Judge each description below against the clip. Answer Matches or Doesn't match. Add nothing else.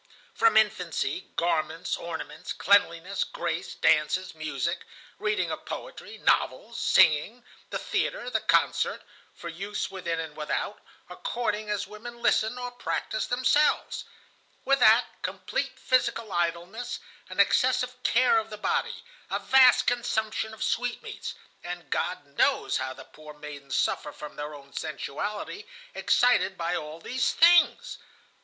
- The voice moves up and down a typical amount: Doesn't match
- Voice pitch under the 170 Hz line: Doesn't match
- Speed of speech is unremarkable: Doesn't match